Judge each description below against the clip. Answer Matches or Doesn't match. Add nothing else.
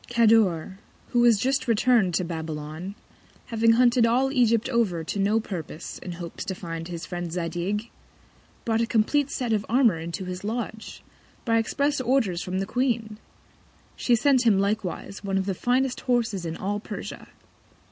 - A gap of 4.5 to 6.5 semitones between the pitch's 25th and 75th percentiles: Matches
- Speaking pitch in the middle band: Doesn't match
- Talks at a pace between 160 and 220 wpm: Matches